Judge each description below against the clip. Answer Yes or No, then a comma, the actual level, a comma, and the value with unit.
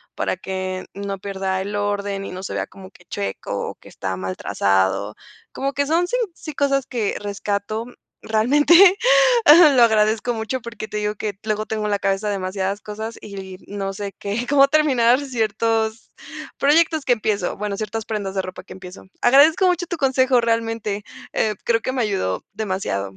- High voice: Yes, high, 215 Hz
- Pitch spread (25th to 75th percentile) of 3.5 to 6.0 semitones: Yes, average, 3.9 semitones